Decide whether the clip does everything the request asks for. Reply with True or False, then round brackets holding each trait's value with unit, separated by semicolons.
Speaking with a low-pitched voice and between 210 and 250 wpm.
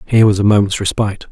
True (100 Hz; 230 wpm)